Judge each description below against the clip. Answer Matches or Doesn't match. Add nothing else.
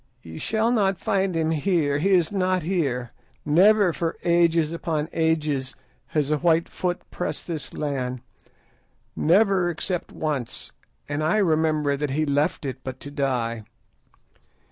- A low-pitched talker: Doesn't match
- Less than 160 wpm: Matches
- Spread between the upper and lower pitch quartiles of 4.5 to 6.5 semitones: Doesn't match